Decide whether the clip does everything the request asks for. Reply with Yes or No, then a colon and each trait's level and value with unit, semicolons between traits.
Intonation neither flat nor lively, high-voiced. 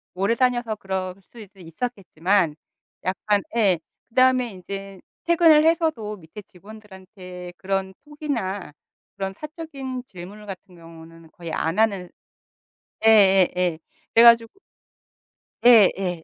Yes: average, 4.3 semitones; high, 195 Hz